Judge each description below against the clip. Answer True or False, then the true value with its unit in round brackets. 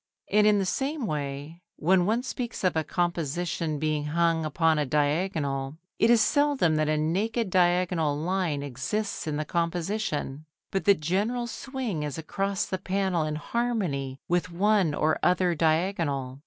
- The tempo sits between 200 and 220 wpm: False (155 wpm)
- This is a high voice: False (170 Hz)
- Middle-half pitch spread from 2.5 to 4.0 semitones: False (4.6 semitones)